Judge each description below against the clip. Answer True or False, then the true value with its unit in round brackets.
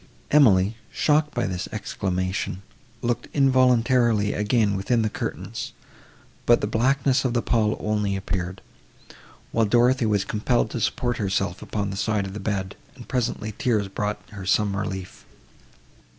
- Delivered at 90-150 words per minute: True (145 wpm)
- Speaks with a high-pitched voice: False (105 Hz)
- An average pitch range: True (3.6 semitones)